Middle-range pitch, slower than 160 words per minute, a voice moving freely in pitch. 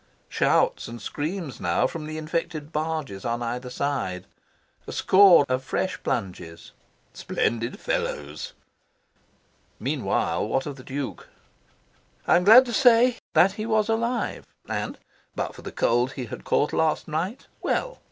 Yes: medium, 150 Hz; average, 140 wpm; wide, 7.9 semitones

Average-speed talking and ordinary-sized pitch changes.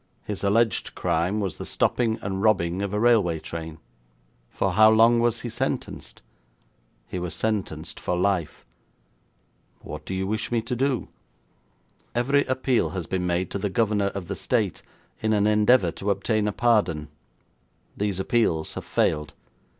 Yes: average, 160 wpm; average, 4.0 semitones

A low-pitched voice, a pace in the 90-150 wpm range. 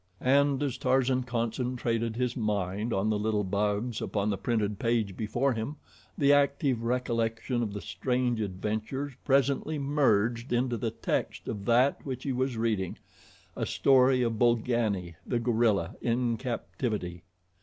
Yes: low, 120 Hz; average, 145 wpm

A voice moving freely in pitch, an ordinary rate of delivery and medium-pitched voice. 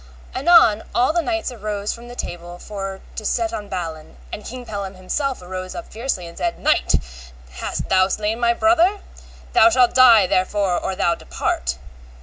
No: wide, 5.7 semitones; average, 170 wpm; high, 210 Hz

